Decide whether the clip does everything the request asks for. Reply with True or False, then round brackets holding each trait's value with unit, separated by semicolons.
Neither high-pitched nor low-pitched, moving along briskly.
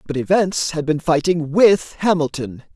False (160 Hz; 150 wpm)